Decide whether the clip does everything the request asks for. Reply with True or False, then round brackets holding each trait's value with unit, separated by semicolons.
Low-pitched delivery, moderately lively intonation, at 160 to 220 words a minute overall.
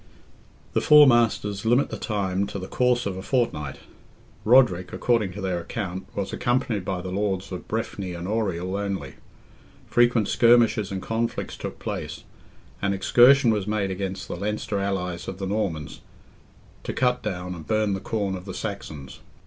True (100 Hz; 3.3 semitones; 165 wpm)